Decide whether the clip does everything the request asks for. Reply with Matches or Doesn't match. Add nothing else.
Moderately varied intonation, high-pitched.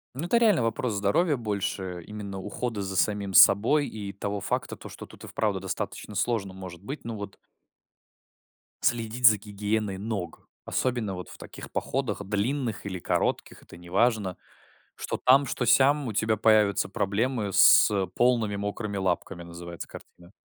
Doesn't match